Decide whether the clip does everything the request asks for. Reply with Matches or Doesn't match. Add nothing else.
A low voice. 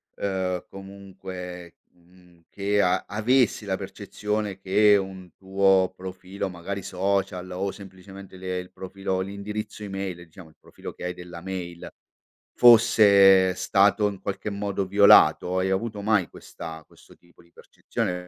Matches